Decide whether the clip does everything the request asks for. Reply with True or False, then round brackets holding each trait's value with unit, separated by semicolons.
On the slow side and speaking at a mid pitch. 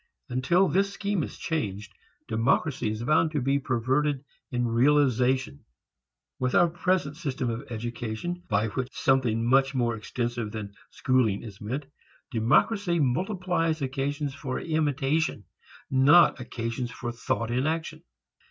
False (130 wpm; 130 Hz)